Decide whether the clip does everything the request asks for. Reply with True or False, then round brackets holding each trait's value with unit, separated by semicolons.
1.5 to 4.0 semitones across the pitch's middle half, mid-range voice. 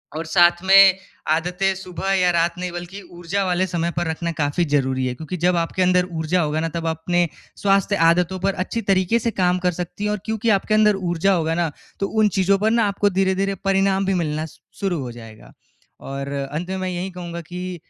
True (2.7 semitones; 180 Hz)